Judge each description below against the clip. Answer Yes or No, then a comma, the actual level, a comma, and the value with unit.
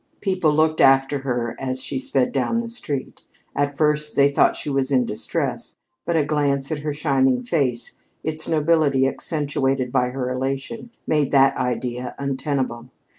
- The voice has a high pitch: No, medium, 140 Hz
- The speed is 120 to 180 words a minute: Yes, average, 160 wpm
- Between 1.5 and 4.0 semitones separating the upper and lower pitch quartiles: Yes, narrow, 2.6 semitones